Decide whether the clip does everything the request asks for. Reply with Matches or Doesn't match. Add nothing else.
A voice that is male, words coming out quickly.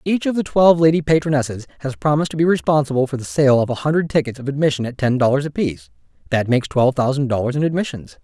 Matches